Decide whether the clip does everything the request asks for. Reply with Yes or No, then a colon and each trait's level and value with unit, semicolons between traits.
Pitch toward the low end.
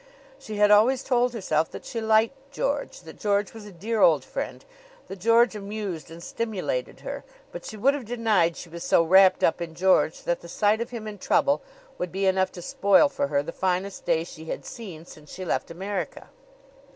No: high, 200 Hz